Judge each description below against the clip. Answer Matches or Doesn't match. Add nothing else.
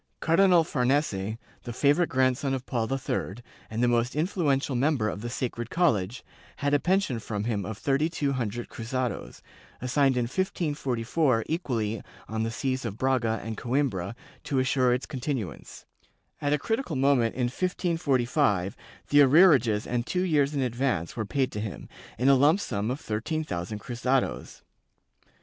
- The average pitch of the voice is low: Matches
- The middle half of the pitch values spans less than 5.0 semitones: Matches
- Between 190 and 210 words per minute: Doesn't match